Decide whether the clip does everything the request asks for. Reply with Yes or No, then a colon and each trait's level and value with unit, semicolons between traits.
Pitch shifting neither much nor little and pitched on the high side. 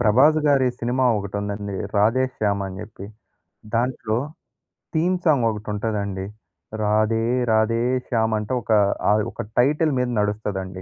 No: average, 3.6 semitones; low, 110 Hz